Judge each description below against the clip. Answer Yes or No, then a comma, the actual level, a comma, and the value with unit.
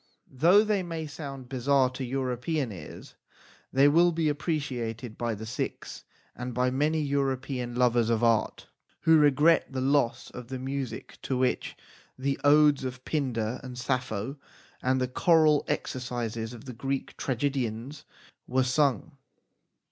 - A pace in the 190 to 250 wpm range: No, average, 140 wpm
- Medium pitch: No, low, 130 Hz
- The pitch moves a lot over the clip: No, average, 2.9 semitones